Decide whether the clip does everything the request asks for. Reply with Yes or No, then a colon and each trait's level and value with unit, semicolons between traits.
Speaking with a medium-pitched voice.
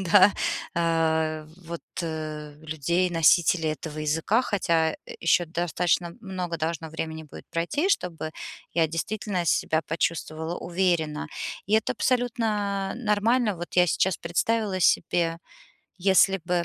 Yes: medium, 170 Hz